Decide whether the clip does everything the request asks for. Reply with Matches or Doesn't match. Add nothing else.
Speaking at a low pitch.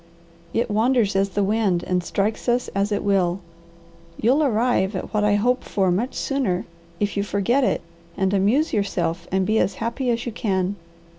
Doesn't match